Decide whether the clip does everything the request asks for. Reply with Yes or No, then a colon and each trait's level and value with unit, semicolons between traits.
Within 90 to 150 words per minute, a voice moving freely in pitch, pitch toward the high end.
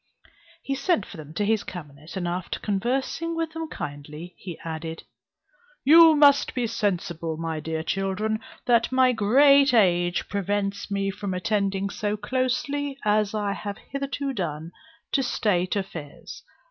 Yes: average, 145 wpm; wide, 6.6 semitones; high, 205 Hz